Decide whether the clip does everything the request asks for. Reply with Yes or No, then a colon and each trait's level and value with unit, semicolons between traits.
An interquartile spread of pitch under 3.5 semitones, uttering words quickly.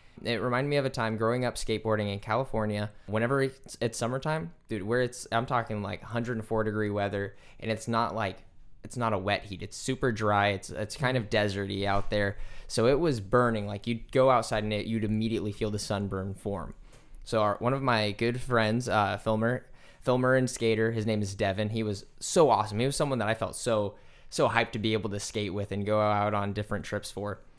Yes: narrow, 2.5 semitones; fast, 220 wpm